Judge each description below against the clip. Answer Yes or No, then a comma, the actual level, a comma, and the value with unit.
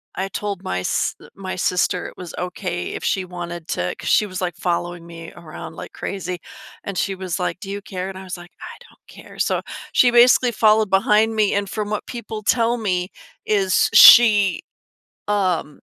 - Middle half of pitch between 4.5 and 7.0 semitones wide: No, average, 2.9 semitones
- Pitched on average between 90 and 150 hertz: No, high, 190 Hz